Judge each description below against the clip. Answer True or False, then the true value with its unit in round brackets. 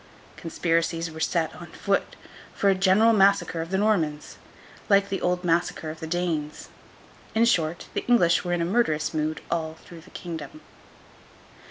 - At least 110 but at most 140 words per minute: False (165 wpm)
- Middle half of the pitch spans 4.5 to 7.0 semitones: False (3.2 semitones)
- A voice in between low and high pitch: True (170 Hz)